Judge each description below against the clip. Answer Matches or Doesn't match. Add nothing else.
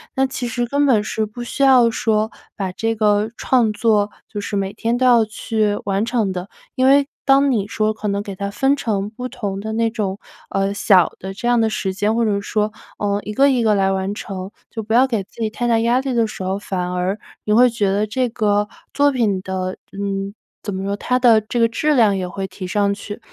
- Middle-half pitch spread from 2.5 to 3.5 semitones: Matches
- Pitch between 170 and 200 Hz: Doesn't match